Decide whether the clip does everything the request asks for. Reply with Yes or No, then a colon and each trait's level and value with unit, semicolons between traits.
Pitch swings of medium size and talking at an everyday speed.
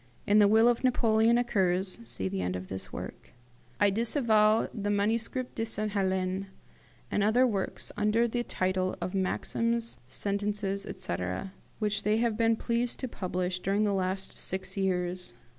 Yes: average, 3.3 semitones; average, 160 wpm